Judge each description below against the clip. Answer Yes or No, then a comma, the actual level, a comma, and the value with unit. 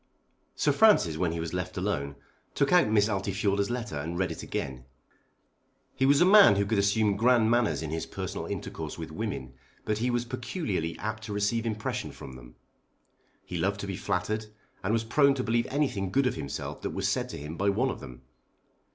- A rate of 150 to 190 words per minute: No, average, 200 wpm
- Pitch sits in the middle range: No, low, 100 Hz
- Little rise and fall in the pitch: No, average, 4.8 semitones